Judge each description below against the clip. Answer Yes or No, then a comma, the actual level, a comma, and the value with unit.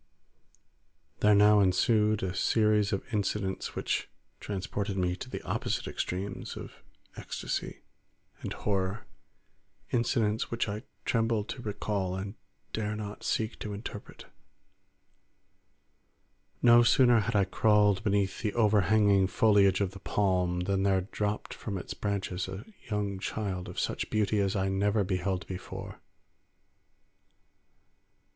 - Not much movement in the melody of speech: Yes, narrow, 1.9 semitones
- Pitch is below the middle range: Yes, low, 100 Hz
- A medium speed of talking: No, slow, 125 wpm